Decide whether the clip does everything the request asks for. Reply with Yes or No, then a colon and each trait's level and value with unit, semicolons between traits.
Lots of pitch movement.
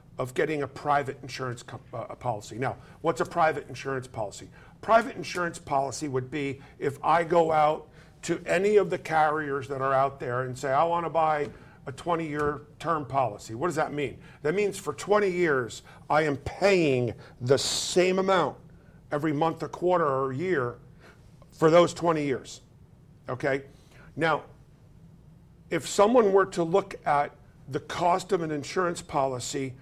No: average, 3.8 semitones